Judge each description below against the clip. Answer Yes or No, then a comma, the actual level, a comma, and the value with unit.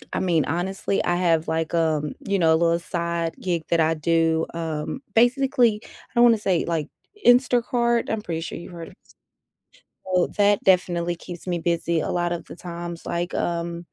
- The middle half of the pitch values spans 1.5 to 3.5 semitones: Yes, average, 2.7 semitones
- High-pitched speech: No, medium, 170 Hz